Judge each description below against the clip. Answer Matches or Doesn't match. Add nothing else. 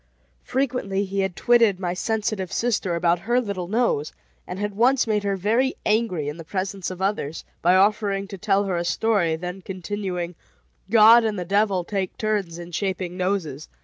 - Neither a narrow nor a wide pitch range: Matches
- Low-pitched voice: Doesn't match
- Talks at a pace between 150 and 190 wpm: Matches